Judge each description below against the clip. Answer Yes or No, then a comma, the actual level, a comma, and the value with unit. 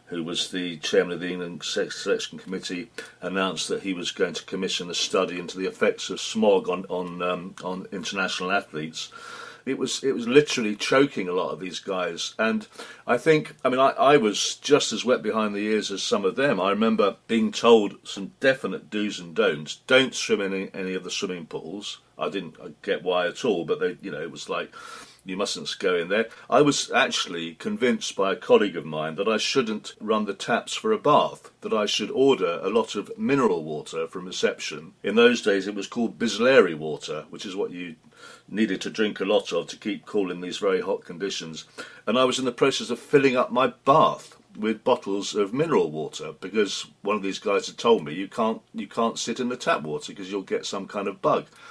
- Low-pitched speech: Yes, low, 120 Hz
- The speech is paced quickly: Yes, fast, 220 wpm